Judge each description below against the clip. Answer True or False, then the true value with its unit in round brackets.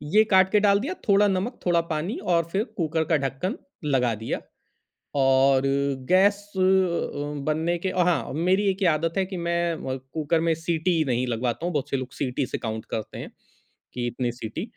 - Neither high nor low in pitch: True (165 Hz)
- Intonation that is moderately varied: False (5.9 semitones)